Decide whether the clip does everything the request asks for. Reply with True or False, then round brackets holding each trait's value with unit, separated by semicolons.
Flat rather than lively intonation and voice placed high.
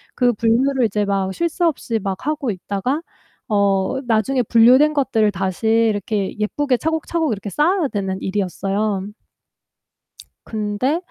False (5.2 semitones; 225 Hz)